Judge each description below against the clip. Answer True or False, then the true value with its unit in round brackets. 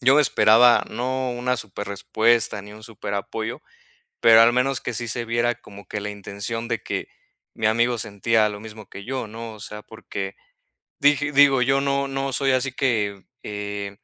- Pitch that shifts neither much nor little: True (3.5 semitones)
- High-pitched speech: False (115 Hz)